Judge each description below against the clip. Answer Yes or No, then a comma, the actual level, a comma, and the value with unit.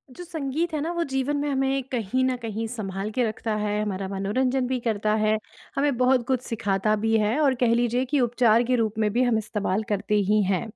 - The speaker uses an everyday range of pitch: Yes, average, 3.6 semitones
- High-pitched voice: Yes, high, 235 Hz